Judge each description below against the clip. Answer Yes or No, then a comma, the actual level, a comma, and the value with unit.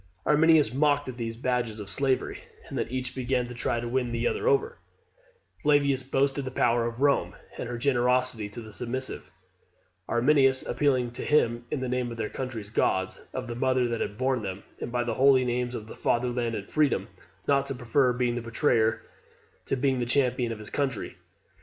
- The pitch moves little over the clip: Yes, narrow, 2.2 semitones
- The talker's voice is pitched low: Yes, low, 125 Hz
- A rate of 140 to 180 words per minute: No, average, 195 wpm